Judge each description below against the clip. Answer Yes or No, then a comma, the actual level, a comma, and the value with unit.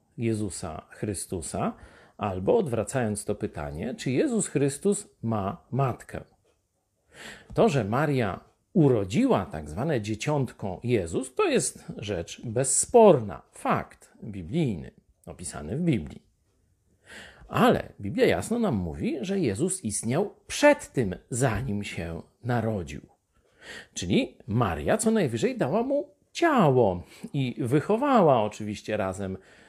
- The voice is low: Yes, low, 125 Hz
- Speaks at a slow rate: Yes, slow, 105 wpm